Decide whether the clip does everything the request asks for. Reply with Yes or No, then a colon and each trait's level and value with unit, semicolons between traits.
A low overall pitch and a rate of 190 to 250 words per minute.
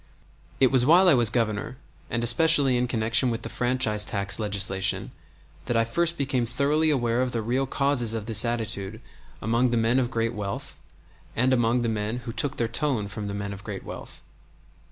Yes: low, 120 Hz; average, 195 wpm